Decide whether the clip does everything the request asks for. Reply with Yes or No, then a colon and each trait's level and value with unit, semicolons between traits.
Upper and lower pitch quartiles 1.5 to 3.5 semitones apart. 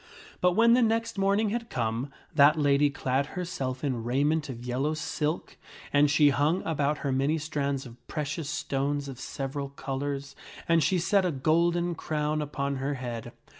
Yes: average, 3.2 semitones